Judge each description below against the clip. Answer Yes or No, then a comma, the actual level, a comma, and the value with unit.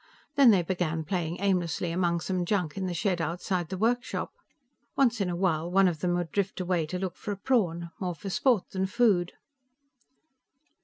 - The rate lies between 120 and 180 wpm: No, average, 190 wpm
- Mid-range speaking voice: Yes, medium, 180 Hz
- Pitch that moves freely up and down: No, narrow, 2.4 semitones